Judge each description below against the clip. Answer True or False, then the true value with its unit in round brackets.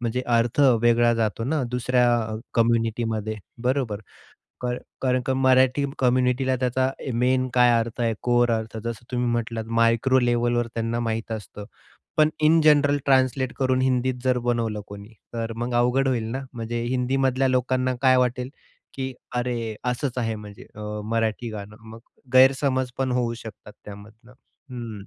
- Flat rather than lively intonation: True (2.2 semitones)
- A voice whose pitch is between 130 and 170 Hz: False (120 Hz)